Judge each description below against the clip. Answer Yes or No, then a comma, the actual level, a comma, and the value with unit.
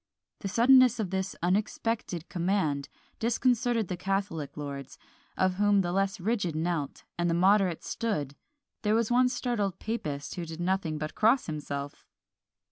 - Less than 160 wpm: Yes, average, 145 wpm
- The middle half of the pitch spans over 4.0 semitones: Yes, average, 5.3 semitones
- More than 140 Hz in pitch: Yes, high, 190 Hz